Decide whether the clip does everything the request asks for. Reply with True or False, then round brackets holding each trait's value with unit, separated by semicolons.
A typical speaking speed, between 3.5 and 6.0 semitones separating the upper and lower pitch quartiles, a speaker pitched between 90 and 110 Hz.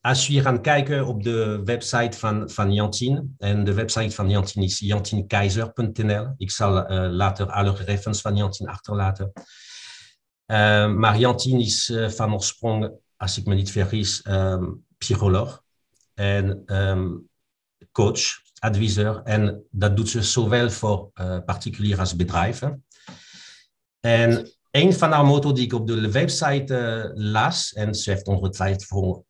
False (145 wpm; 3.0 semitones; 105 Hz)